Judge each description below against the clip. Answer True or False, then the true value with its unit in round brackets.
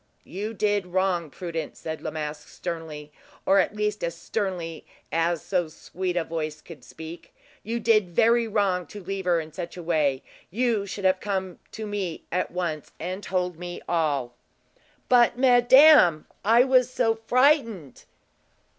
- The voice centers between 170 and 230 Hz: True (185 Hz)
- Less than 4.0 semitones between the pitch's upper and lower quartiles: False (4.4 semitones)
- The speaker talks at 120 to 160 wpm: True (155 wpm)